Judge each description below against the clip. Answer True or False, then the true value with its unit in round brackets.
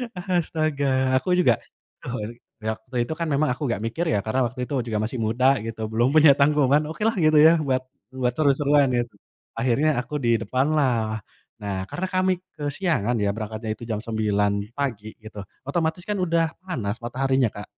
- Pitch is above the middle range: False (130 Hz)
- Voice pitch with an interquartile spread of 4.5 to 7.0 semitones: True (5.5 semitones)